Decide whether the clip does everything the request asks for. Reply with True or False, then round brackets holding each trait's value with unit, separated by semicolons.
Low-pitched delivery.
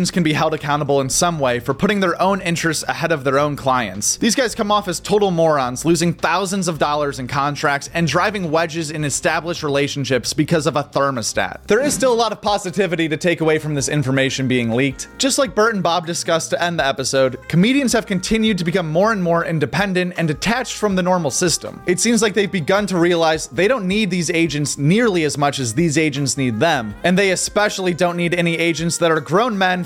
False (170 Hz)